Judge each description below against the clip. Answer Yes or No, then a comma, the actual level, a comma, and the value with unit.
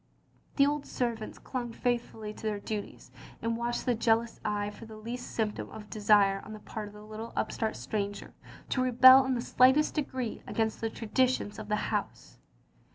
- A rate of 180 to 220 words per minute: Yes, average, 185 wpm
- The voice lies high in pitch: Yes, high, 225 Hz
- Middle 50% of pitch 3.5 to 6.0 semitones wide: No, average, 2.7 semitones